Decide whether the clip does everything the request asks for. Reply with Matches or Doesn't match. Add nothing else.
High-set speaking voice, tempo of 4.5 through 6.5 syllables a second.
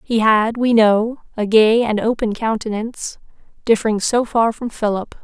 Matches